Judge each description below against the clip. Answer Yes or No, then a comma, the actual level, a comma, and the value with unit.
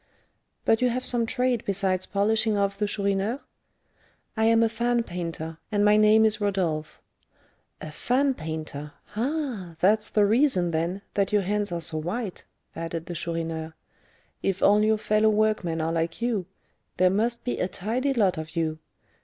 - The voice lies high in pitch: Yes, high, 200 Hz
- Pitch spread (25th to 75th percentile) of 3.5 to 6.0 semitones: Yes, average, 4.7 semitones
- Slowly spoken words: No, average, 165 wpm